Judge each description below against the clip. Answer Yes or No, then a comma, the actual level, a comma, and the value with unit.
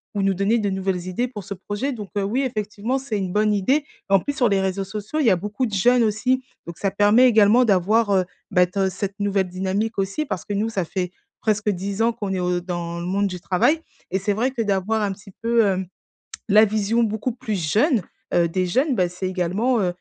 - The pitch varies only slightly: No, average, 3.0 semitones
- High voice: Yes, high, 205 Hz